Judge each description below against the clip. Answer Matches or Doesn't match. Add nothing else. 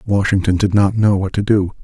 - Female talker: Doesn't match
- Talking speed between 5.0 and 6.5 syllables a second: Matches